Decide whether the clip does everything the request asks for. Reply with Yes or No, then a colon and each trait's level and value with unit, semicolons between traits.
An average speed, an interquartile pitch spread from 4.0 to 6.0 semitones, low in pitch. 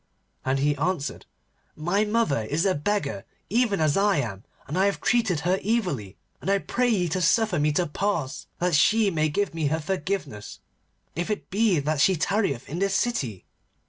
No: average, 185 wpm; wide, 5.5 semitones; medium, 180 Hz